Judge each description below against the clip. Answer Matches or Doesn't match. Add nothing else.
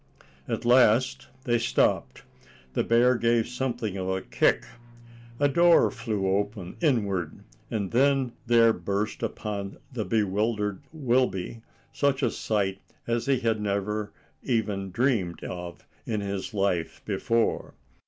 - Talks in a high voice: Doesn't match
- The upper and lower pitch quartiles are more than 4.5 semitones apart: Doesn't match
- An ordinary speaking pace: Doesn't match